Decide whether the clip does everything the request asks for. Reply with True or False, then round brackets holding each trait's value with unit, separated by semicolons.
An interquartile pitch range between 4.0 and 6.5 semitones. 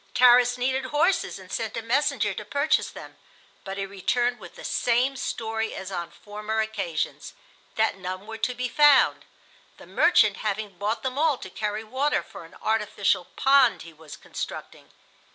True (4.4 semitones)